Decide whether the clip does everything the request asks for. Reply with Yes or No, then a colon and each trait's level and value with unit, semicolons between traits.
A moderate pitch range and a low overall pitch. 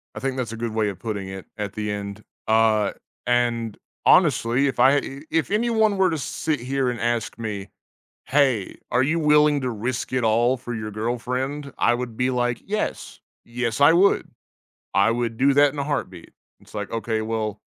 Yes: average, 3.8 semitones; low, 120 Hz